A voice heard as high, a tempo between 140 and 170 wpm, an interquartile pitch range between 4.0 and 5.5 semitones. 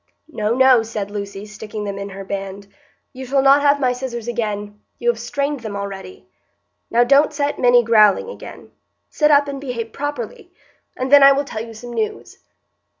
No: high, 240 Hz; average, 180 wpm; average, 5.1 semitones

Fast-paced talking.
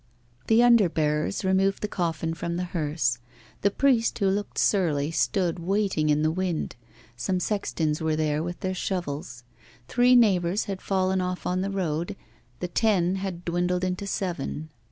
No: average, 160 wpm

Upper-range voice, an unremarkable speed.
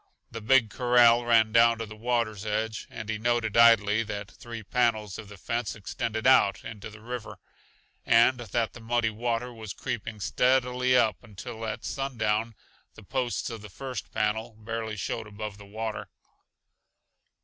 No: low, 115 Hz; average, 160 wpm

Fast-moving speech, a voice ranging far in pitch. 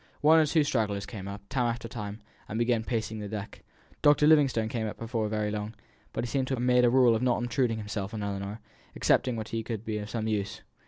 No: fast, 235 wpm; average, 2.7 semitones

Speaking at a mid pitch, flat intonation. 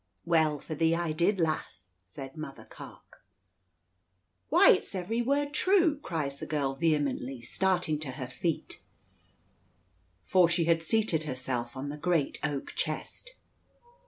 No: medium, 155 Hz; average, 4.3 semitones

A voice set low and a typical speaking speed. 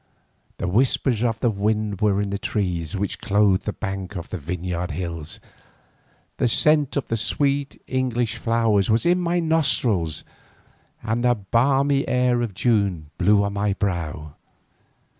Yes: low, 105 Hz; average, 150 wpm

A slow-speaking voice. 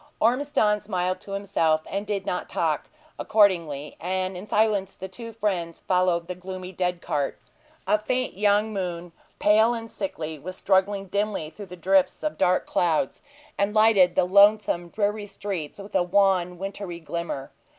No: average, 155 wpm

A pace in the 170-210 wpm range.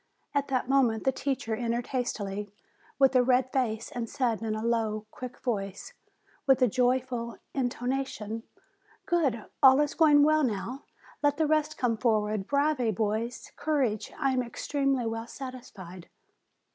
No: average, 155 wpm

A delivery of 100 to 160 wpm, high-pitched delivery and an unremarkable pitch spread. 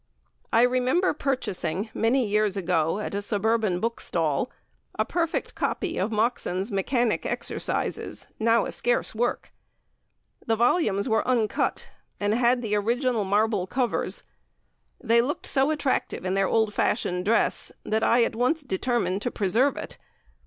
Yes: average, 145 wpm; high, 225 Hz; average, 3.5 semitones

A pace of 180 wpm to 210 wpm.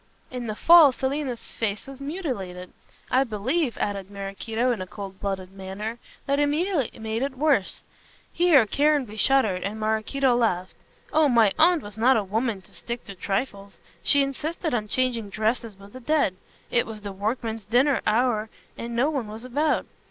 No: average, 170 wpm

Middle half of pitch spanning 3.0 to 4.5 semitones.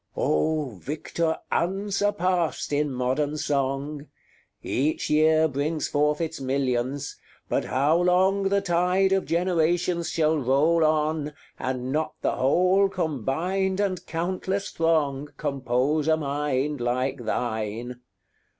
Yes: average, 4.2 semitones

